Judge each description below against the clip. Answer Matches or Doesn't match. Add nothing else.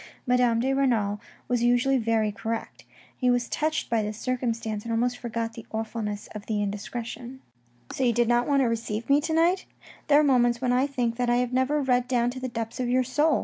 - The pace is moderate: Doesn't match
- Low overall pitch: Doesn't match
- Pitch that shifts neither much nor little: Doesn't match